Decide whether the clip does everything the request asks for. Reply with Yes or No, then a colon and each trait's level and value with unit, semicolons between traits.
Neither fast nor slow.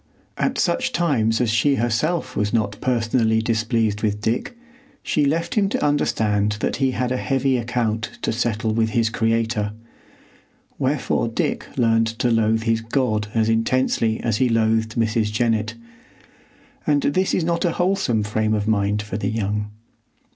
Yes: average, 160 wpm